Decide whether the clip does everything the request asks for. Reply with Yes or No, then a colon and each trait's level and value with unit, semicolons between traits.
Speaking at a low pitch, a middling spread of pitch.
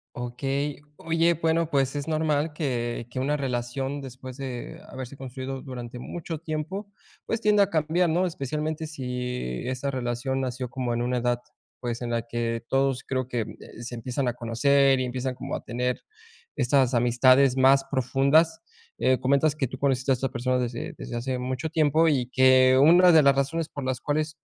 Yes: low, 130 Hz; average, 3.1 semitones